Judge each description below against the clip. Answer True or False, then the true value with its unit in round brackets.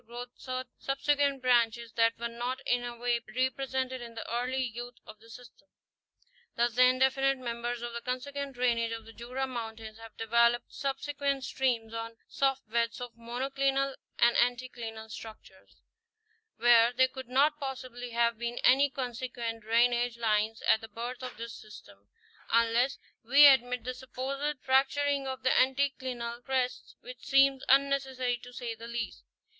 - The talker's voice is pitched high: True (245 Hz)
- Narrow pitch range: True (2.2 semitones)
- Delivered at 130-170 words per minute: True (155 wpm)